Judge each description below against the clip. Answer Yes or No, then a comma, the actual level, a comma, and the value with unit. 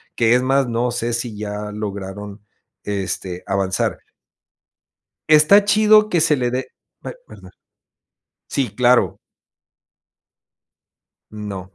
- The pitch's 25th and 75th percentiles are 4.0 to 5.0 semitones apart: Yes, average, 4.4 semitones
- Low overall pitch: Yes, low, 115 Hz